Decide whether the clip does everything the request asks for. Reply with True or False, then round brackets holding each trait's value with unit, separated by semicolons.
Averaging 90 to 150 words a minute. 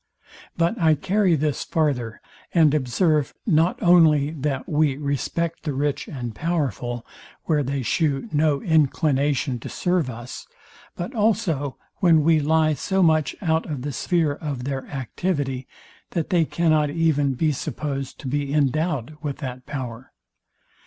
True (145 wpm)